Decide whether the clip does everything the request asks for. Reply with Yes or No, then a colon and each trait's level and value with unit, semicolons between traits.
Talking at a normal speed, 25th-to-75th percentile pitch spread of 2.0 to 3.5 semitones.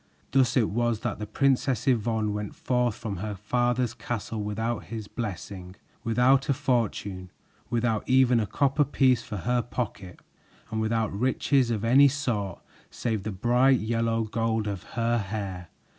Yes: average, 155 wpm; average, 2.8 semitones